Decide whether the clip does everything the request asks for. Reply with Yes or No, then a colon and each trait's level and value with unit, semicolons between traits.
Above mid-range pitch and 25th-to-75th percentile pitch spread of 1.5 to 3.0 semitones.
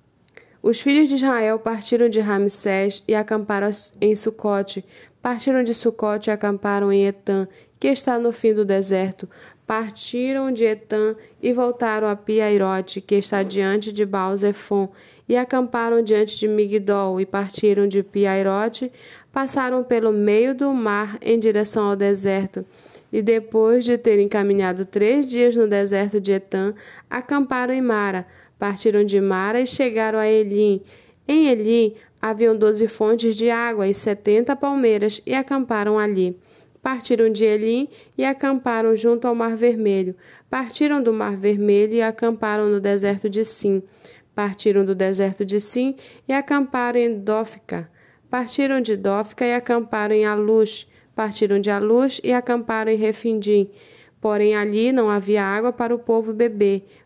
Yes: high, 215 Hz; average, 2.7 semitones